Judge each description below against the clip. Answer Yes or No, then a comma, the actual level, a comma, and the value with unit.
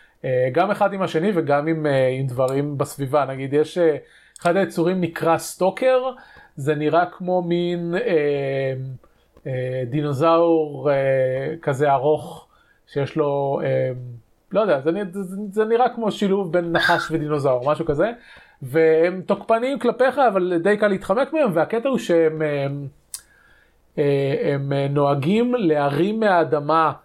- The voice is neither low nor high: Yes, medium, 160 Hz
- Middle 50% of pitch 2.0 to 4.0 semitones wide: No, average, 5.1 semitones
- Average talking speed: Yes, average, 140 wpm